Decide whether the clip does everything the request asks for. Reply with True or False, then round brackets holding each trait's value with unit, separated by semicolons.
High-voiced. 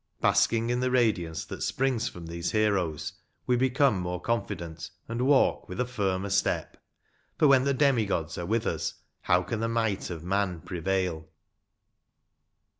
False (100 Hz)